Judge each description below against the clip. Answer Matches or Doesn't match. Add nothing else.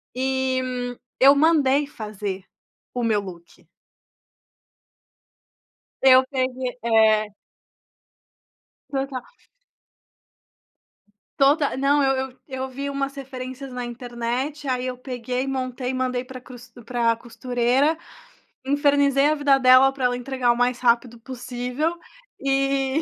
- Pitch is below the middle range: Doesn't match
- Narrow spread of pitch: Matches